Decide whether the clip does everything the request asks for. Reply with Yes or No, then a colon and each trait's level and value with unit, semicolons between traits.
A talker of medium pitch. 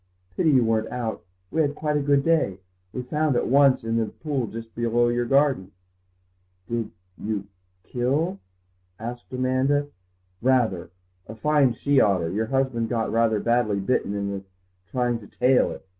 No: low, 120 Hz